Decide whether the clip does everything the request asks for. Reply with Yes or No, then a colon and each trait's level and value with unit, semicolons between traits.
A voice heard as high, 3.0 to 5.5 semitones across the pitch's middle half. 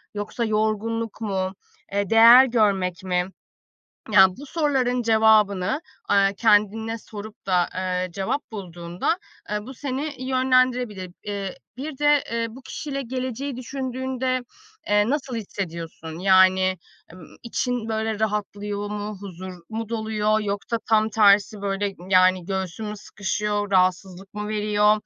Yes: high, 210 Hz; average, 3.4 semitones